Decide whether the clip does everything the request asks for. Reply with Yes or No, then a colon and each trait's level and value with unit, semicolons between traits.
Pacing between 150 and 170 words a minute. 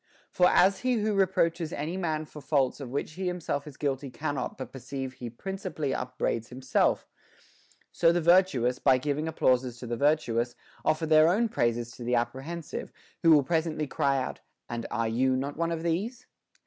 No: average, 180 wpm